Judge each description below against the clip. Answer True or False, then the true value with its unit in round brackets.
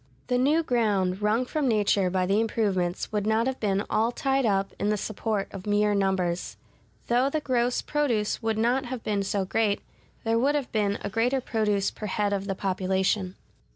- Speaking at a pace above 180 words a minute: True (190 wpm)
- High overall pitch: True (210 Hz)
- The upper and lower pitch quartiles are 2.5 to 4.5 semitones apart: True (3.5 semitones)